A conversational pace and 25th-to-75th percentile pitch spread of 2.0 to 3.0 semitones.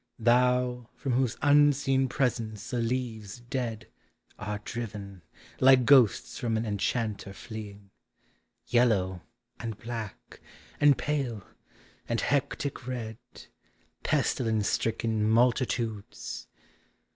No: slow, 95 wpm; average, 2.7 semitones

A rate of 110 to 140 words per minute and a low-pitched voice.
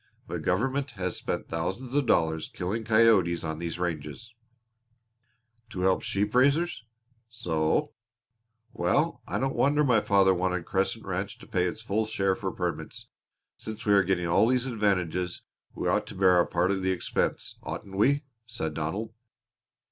No: average, 165 wpm; very low, 95 Hz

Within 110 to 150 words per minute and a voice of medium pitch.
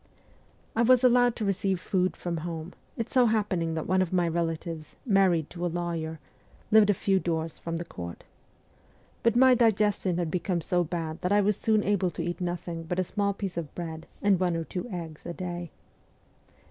No: average, 200 wpm; medium, 180 Hz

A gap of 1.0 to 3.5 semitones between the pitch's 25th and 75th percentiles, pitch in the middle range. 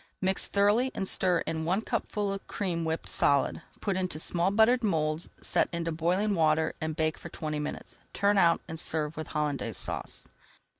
No: average, 3.9 semitones; medium, 170 Hz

